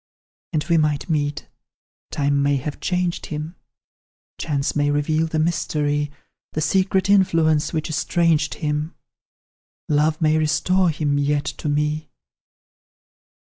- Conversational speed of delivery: No, slow, 120 wpm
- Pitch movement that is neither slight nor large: No, narrow, 1.8 semitones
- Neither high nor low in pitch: Yes, medium, 155 Hz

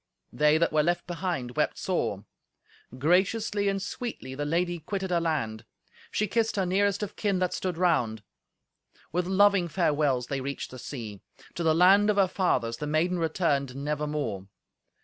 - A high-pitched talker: No, medium, 170 Hz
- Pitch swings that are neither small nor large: Yes, average, 4.9 semitones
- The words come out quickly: No, average, 165 wpm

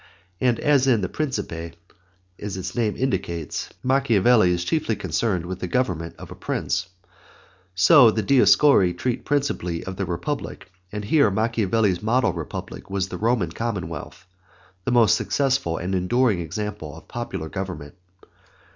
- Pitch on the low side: Yes, low, 105 Hz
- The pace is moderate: Yes, average, 145 wpm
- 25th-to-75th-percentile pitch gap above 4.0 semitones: Yes, wide, 5.6 semitones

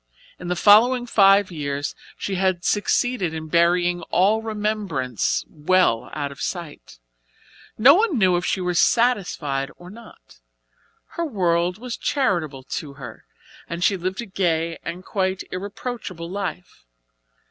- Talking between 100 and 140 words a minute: Yes, slow, 135 wpm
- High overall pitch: No, medium, 180 Hz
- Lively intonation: No, average, 4.0 semitones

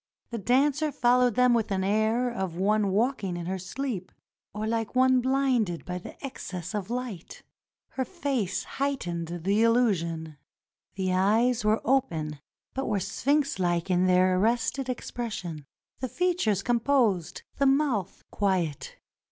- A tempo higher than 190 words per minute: No, average, 140 wpm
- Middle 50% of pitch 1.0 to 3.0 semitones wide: No, wide, 5.5 semitones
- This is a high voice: Yes, high, 220 Hz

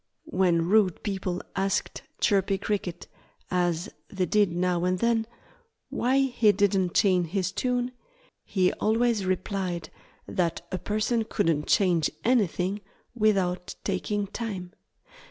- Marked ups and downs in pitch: No, average, 3.0 semitones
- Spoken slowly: Yes, slow, 120 wpm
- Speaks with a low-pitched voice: No, high, 190 Hz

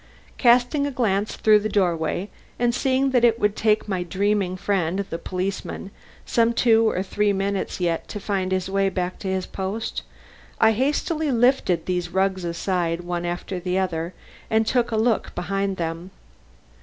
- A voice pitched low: No, high, 195 Hz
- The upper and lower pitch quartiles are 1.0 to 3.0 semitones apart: No, average, 3.6 semitones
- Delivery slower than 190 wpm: Yes, average, 170 wpm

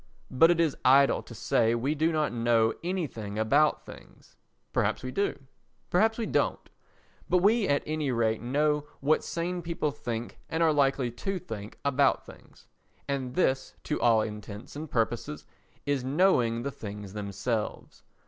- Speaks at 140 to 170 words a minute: Yes, average, 150 wpm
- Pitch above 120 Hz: Yes, low, 135 Hz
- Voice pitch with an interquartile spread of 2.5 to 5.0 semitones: No, wide, 5.4 semitones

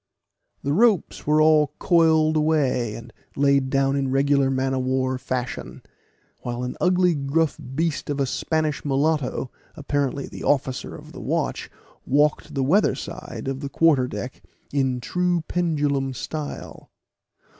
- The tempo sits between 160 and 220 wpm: No, average, 140 wpm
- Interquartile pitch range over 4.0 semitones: No, average, 2.9 semitones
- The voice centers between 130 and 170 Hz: Yes, medium, 140 Hz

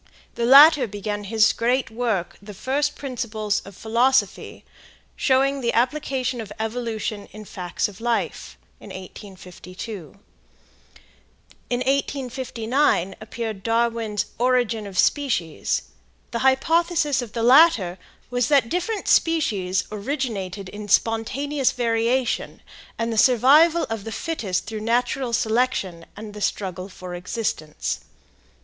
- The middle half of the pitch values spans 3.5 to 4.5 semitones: Yes, average, 4.1 semitones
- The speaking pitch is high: Yes, high, 230 Hz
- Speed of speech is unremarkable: No, slow, 120 wpm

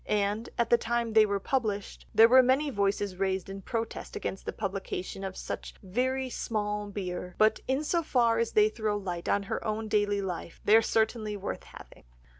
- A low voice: No, high, 210 Hz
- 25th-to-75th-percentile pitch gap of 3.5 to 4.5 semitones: No, average, 2.8 semitones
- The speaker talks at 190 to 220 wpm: Yes, average, 195 wpm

